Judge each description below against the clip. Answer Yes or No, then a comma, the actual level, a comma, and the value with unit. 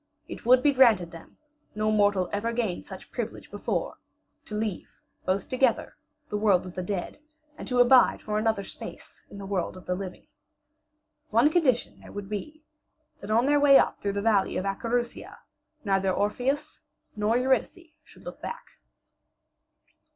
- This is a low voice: No, high, 215 Hz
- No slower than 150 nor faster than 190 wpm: Yes, average, 165 wpm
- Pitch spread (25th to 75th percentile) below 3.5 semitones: No, average, 4.2 semitones